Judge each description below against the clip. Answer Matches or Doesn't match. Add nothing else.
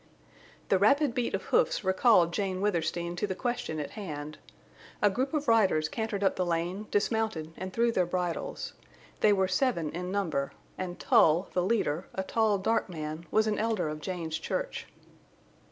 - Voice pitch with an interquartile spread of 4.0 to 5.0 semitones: Matches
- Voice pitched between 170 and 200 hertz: Matches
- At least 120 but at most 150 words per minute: Doesn't match